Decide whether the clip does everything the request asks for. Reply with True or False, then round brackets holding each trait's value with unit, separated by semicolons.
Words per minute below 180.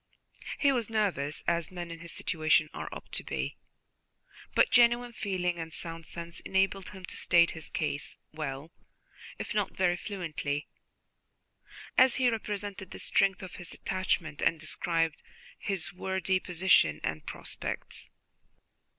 True (140 wpm)